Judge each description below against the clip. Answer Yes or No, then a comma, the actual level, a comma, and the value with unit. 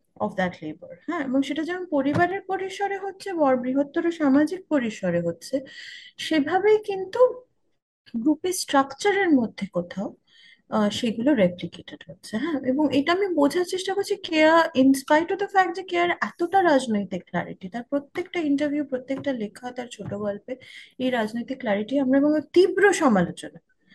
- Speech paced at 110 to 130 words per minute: No, fast, 140 wpm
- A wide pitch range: Yes, wide, 7.6 semitones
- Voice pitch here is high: Yes, very high, 280 Hz